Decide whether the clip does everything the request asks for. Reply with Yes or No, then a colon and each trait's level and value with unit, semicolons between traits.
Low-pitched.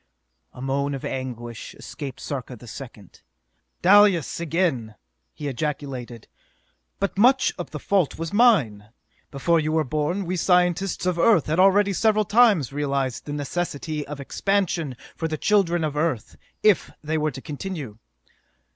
No: medium, 155 Hz